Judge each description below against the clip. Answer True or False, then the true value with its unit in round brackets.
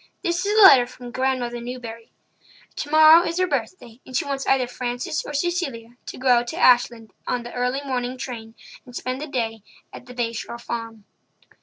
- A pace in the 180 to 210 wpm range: True (190 wpm)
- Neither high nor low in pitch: False (250 Hz)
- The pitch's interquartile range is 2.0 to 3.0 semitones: True (2.7 semitones)